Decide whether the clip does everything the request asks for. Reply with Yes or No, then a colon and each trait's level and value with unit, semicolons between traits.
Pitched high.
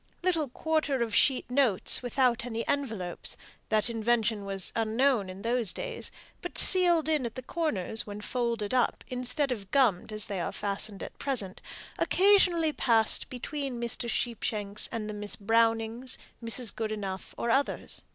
Yes: high, 235 Hz